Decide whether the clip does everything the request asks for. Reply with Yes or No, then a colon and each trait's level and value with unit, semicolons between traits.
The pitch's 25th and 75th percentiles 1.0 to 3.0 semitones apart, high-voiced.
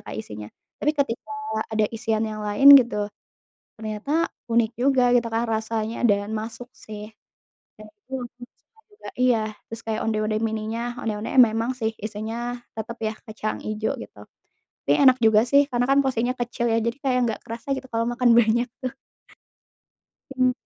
Yes: narrow, 2.4 semitones; high, 230 Hz